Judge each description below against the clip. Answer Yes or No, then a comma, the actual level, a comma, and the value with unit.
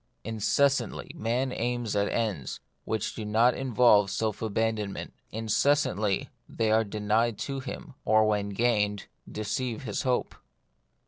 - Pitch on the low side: Yes, low, 110 Hz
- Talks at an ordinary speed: No, slow, 130 wpm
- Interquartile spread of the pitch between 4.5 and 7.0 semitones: No, narrow, 2.6 semitones